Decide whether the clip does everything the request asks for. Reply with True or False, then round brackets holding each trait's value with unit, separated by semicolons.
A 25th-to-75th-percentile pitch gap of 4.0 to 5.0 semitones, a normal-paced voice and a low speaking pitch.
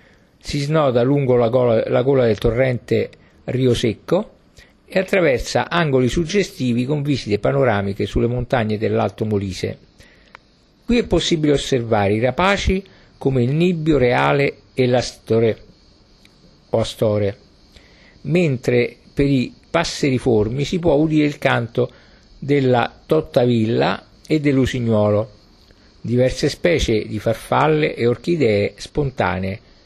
False (4.7 semitones; 110 wpm; 125 Hz)